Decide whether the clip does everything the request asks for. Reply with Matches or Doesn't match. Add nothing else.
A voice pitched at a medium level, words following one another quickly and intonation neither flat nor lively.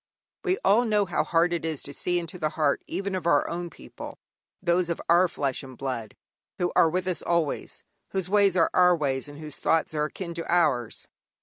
Matches